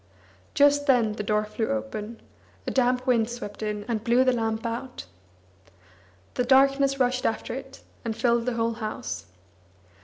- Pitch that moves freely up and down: No, average, 2.8 semitones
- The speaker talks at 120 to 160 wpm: Yes, average, 155 wpm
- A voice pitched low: No, high, 235 Hz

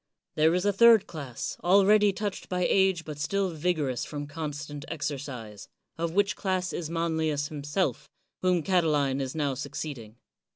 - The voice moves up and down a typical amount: Yes, average, 4.2 semitones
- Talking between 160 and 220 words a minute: No, average, 150 wpm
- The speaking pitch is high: No, medium, 160 Hz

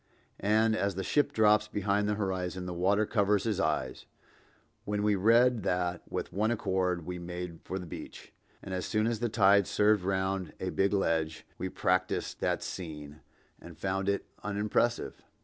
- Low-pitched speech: Yes, very low, 95 Hz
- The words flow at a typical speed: Yes, average, 165 wpm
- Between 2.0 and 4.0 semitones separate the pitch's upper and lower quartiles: Yes, narrow, 2.5 semitones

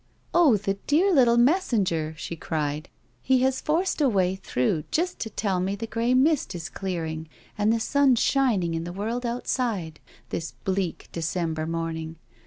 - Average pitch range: No, wide, 7.4 semitones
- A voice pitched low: No, high, 200 Hz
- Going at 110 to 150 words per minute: No, average, 170 wpm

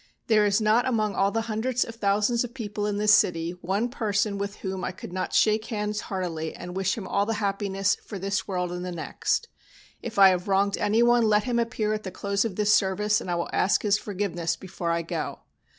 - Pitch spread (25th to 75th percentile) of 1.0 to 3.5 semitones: Yes, narrow, 2.4 semitones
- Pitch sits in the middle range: No, high, 205 Hz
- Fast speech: Yes, fast, 225 wpm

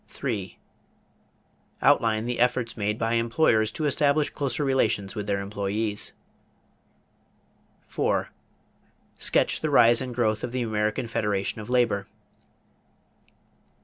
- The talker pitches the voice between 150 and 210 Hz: No, low, 115 Hz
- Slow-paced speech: Yes, slow, 115 wpm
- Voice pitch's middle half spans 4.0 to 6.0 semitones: No, average, 2.9 semitones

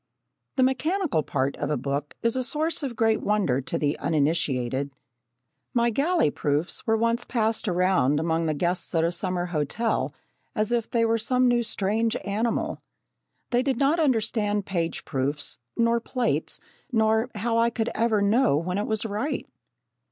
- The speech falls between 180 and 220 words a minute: No, average, 165 wpm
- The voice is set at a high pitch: Yes, high, 215 Hz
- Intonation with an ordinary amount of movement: No, wide, 6.2 semitones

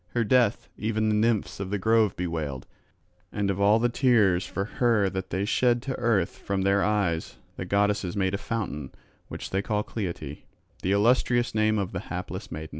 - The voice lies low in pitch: Yes, low, 100 Hz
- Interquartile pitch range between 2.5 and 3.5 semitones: Yes, average, 3.1 semitones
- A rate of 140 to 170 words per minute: No, average, 190 wpm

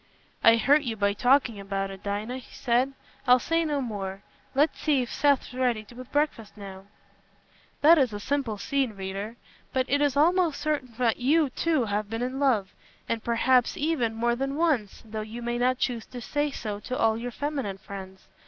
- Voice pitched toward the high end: Yes, high, 245 Hz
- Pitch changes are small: No, average, 4.6 semitones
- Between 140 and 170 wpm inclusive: No, average, 185 wpm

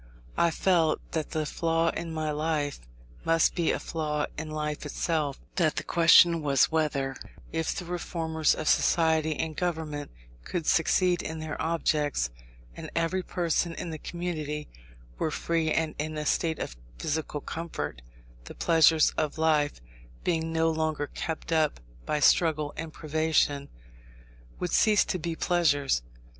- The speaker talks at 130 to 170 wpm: Yes, average, 150 wpm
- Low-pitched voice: No, medium, 160 Hz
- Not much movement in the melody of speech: Yes, narrow, 1.6 semitones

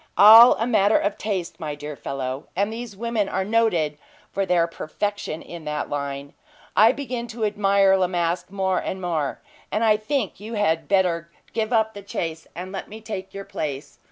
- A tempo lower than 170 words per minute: No, average, 185 wpm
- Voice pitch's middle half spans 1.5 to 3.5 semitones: No, average, 4.6 semitones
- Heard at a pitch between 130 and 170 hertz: No, high, 195 Hz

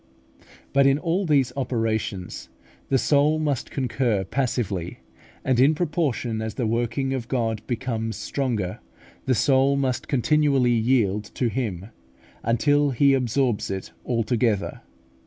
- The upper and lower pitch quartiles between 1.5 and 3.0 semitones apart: No, average, 3.6 semitones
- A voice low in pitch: Yes, low, 125 Hz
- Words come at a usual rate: No, slow, 125 wpm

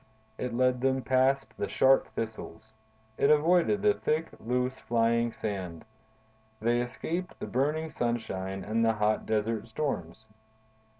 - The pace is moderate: No, slow, 130 wpm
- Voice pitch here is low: Yes, low, 120 Hz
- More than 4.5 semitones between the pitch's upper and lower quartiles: No, average, 3.6 semitones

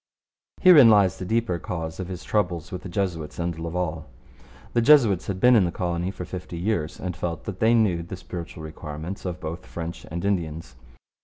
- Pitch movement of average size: Yes, average, 3.1 semitones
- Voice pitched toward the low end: Yes, very low, 90 Hz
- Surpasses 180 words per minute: Yes, average, 190 wpm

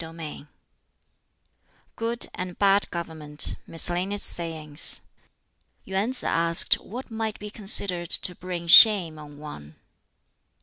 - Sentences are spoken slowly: Yes, slow, 115 wpm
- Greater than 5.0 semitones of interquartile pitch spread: No, average, 3.9 semitones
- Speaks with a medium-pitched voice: Yes, medium, 175 Hz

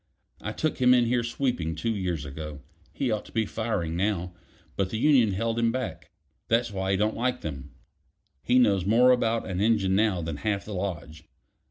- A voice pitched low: Yes, low, 105 Hz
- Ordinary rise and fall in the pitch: Yes, average, 4.5 semitones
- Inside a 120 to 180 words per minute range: No, average, 195 wpm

